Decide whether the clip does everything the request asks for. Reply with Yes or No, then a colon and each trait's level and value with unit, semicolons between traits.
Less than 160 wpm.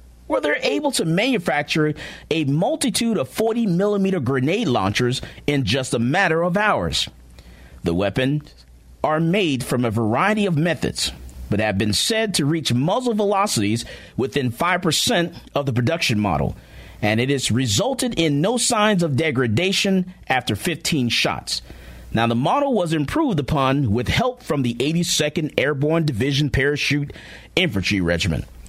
Yes: average, 145 wpm